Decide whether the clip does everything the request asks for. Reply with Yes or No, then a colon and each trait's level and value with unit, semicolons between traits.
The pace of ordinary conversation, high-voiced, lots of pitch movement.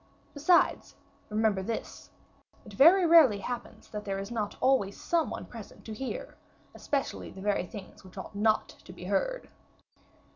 Yes: average, 155 wpm; high, 220 Hz; wide, 6.5 semitones